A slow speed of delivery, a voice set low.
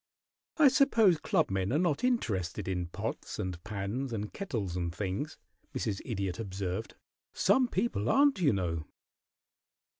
Yes: slow, 130 wpm; low, 105 Hz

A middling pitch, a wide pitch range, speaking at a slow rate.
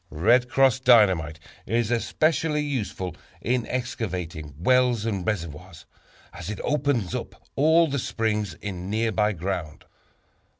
No: low, 110 Hz; wide, 5.8 semitones; slow, 120 wpm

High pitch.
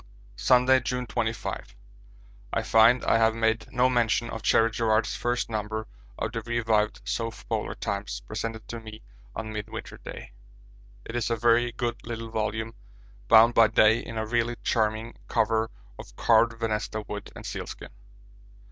No: low, 115 Hz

